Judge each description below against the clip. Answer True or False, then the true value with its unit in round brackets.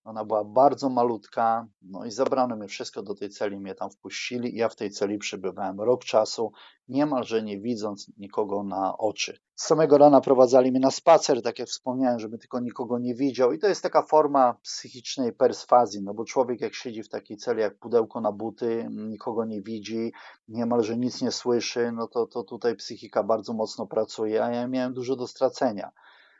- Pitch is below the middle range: True (120 Hz)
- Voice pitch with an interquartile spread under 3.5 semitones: True (2.6 semitones)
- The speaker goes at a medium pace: False (190 wpm)